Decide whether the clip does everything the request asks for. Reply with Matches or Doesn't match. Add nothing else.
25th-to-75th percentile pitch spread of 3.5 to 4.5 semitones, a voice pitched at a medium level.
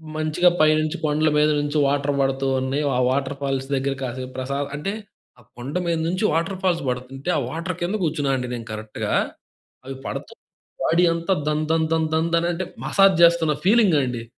Matches